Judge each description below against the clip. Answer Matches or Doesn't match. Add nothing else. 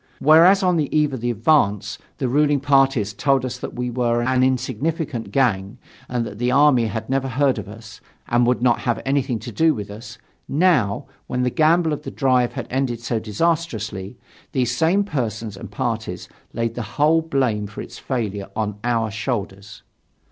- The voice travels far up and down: Doesn't match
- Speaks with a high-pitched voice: Doesn't match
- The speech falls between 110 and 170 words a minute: Doesn't match